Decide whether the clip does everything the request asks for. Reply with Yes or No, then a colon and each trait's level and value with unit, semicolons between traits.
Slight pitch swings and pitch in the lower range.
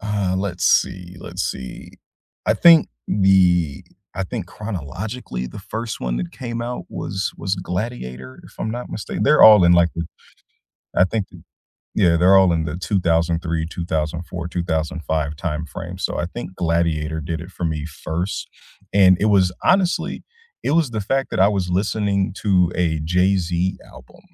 No: average, 3.3 semitones; very low, 90 Hz